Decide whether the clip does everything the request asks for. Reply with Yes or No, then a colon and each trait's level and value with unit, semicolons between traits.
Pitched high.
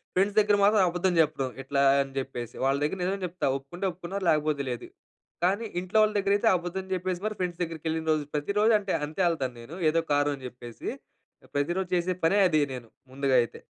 No: medium, 170 Hz